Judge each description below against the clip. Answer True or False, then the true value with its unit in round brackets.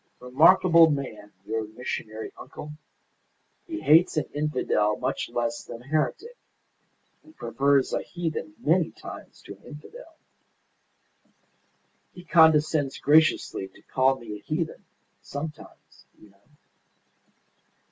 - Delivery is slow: True (115 wpm)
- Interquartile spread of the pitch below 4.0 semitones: False (5.3 semitones)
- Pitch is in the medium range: True (150 Hz)